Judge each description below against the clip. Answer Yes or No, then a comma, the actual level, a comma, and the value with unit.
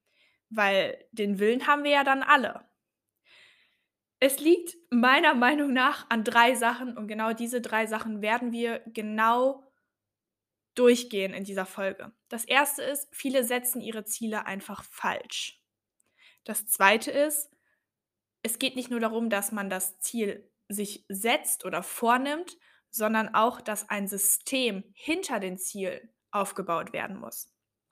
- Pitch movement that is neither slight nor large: Yes, average, 3.8 semitones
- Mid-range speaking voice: No, high, 230 Hz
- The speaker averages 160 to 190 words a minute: No, average, 140 wpm